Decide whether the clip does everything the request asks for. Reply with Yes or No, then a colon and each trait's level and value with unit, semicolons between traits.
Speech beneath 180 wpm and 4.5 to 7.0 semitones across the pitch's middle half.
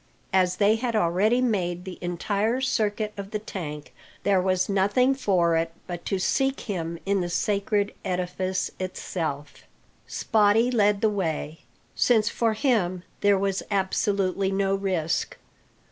No: average, 140 wpm; average, 2.9 semitones